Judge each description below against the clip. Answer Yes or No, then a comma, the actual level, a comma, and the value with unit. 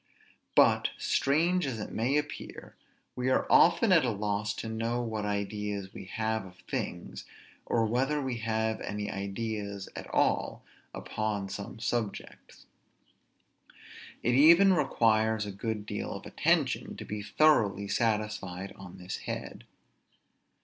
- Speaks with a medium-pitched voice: No, low, 110 Hz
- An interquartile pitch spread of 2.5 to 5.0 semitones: Yes, average, 3.1 semitones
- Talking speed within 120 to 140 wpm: Yes, slow, 135 wpm